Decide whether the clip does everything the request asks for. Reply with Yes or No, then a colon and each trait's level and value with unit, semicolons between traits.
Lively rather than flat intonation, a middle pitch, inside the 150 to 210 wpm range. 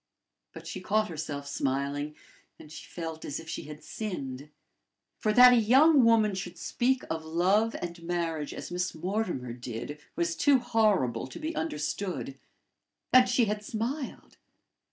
Yes: wide, 6.8 semitones; medium, 175 Hz; average, 155 wpm